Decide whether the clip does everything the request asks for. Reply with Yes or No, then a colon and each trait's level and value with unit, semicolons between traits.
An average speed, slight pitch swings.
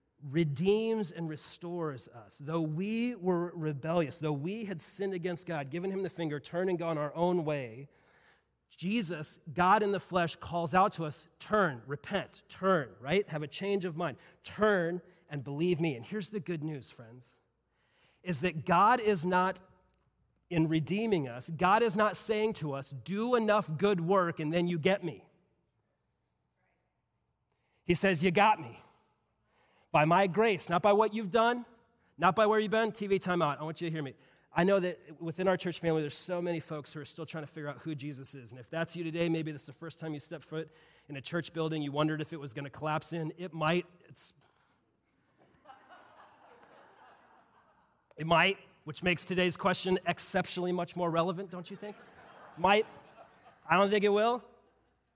No: average, 185 wpm; average, 3.8 semitones